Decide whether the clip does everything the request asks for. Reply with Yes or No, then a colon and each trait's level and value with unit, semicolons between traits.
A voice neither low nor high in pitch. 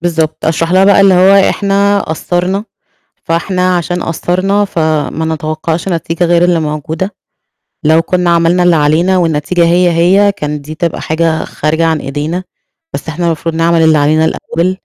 Yes: medium, 170 Hz